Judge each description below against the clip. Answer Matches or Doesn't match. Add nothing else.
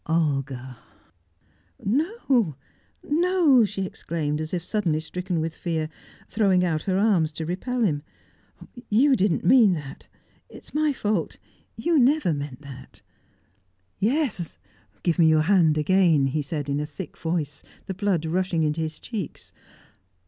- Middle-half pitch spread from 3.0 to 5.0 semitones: Doesn't match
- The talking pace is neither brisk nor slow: Matches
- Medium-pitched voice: Matches